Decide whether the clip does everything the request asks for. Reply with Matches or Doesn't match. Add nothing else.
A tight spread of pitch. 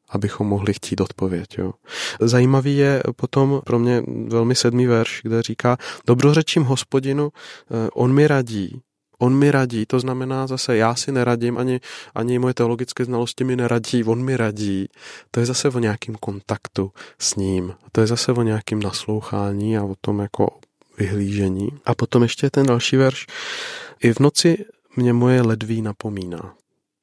Doesn't match